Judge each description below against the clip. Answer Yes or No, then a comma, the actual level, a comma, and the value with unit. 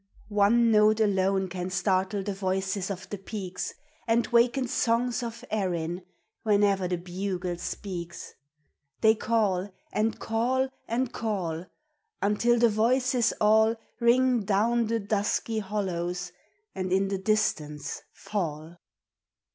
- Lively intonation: No, average, 3.4 semitones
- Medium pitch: No, high, 205 Hz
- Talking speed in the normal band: No, slow, 120 wpm